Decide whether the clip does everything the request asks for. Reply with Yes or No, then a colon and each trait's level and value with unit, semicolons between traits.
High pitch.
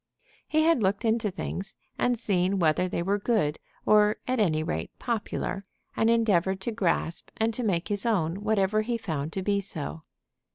Yes: high, 200 Hz